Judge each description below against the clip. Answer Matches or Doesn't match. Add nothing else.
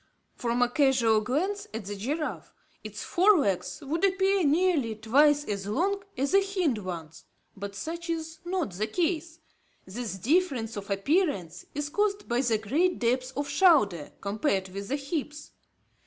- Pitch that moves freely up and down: Matches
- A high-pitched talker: Matches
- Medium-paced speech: Matches